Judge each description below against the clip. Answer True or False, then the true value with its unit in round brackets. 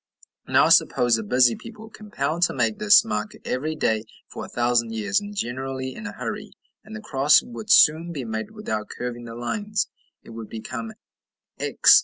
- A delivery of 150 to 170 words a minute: False (180 wpm)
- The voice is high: False (135 Hz)